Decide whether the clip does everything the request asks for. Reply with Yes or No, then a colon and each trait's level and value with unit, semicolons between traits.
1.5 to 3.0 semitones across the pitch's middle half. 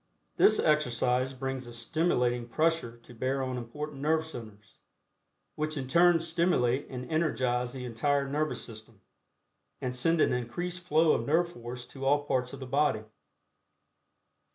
No: average, 4.1 semitones